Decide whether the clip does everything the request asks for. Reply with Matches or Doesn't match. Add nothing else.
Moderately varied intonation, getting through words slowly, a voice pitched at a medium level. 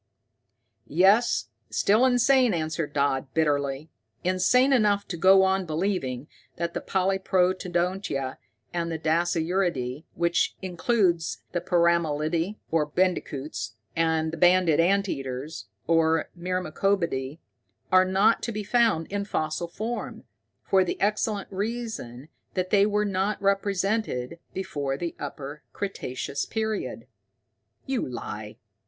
Matches